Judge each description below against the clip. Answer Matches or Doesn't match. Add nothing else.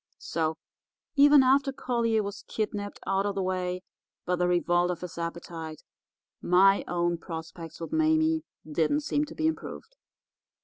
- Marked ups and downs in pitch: Matches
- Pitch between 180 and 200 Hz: Matches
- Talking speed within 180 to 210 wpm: Doesn't match